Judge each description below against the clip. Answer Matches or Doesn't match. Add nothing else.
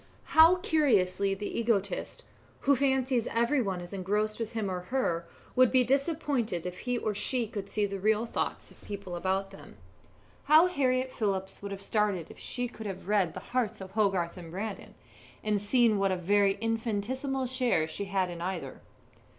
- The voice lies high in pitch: Matches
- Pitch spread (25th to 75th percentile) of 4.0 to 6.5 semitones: Matches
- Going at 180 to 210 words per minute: Matches